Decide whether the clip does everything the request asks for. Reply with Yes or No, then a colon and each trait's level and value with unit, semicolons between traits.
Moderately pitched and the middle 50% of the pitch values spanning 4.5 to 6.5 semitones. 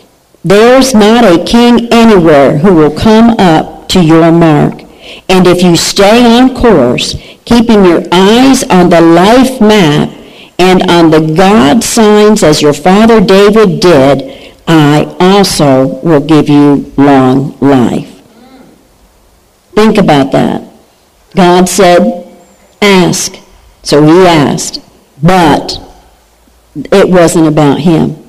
Yes: medium, 180 Hz; average, 5.1 semitones